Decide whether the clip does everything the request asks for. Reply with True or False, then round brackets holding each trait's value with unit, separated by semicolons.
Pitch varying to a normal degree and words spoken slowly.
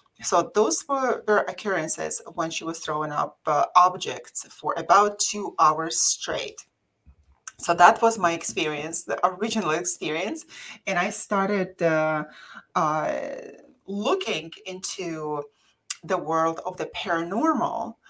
True (4.6 semitones; 125 wpm)